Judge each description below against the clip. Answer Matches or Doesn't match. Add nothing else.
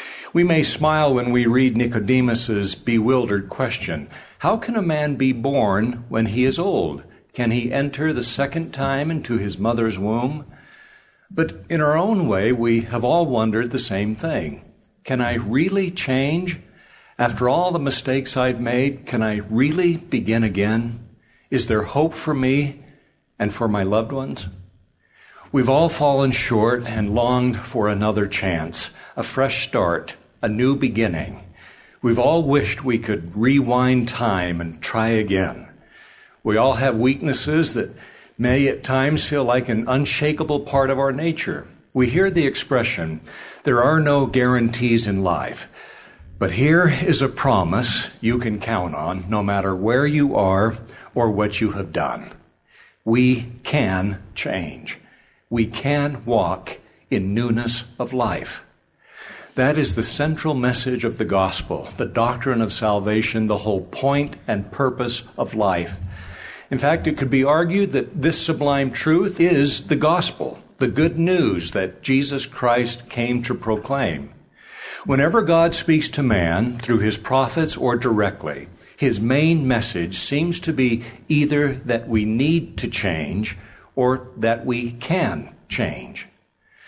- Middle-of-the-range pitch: Doesn't match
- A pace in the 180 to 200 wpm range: Doesn't match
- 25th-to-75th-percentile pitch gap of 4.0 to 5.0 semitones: Matches